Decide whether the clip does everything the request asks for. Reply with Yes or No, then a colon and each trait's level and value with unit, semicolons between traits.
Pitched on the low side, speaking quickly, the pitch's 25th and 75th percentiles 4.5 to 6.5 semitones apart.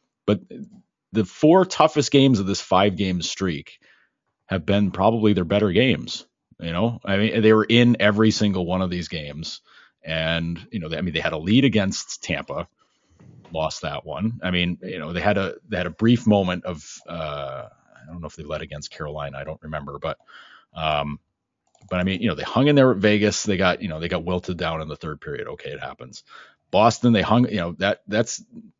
Yes: very low, 95 Hz; fast, 215 wpm; average, 4.9 semitones